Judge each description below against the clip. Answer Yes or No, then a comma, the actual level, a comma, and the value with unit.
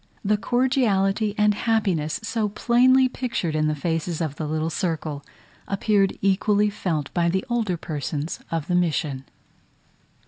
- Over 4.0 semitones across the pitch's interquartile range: Yes, average, 5.2 semitones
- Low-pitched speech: No, high, 190 Hz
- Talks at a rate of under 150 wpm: Yes, average, 140 wpm